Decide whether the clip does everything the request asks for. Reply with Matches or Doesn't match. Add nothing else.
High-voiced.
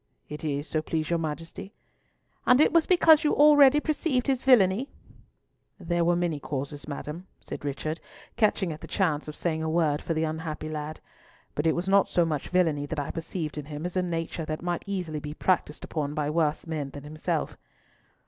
Doesn't match